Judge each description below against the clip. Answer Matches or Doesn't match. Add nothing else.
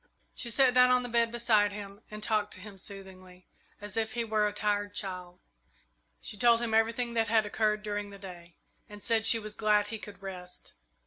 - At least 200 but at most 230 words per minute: Matches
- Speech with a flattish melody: Matches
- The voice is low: Doesn't match